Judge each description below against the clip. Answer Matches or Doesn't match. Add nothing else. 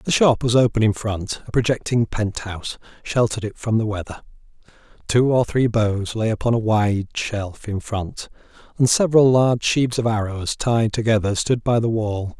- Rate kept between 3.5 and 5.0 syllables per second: Matches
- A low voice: Matches